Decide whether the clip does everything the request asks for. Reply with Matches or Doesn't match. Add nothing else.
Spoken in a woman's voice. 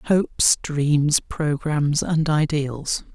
Doesn't match